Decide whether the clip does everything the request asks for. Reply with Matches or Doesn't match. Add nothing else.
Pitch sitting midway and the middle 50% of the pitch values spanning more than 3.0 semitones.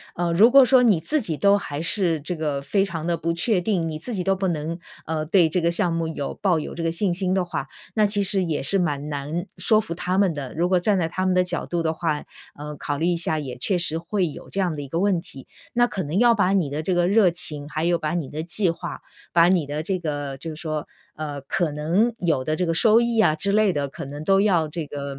Matches